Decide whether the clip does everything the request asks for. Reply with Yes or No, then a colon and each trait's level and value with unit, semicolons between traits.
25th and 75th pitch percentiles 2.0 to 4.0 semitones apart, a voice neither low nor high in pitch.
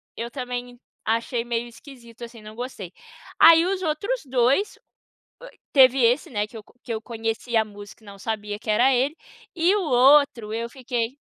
No: average, 3.2 semitones; high, 240 Hz